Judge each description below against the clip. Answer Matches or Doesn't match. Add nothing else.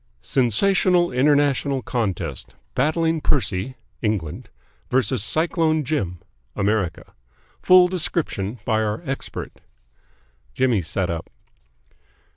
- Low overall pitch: Matches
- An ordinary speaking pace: Doesn't match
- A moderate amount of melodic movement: Doesn't match